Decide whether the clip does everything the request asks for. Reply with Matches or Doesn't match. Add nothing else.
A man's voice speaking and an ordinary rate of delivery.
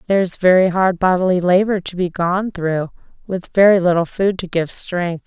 Doesn't match